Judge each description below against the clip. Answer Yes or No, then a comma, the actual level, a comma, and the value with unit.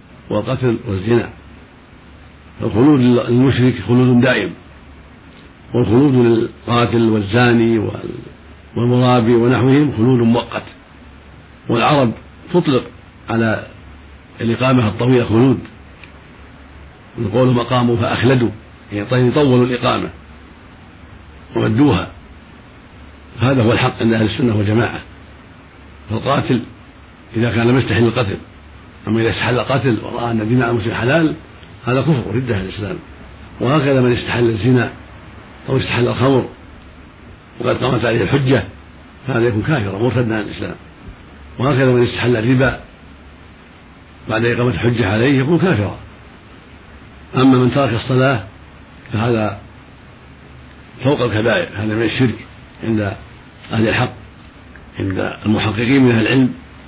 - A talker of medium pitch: No, low, 115 Hz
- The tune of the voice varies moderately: Yes, average, 4.9 semitones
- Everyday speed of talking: Yes, average, 100 wpm